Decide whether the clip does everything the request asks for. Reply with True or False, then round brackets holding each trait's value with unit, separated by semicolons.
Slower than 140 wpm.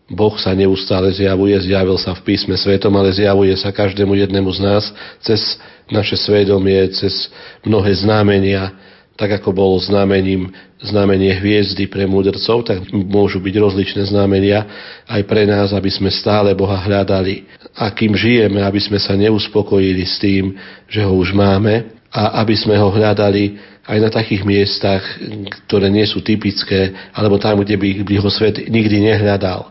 False (155 wpm)